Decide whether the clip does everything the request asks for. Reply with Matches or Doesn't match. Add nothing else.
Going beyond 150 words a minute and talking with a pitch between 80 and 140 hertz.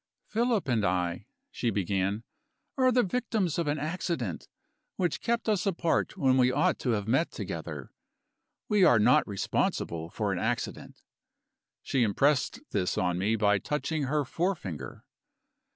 Doesn't match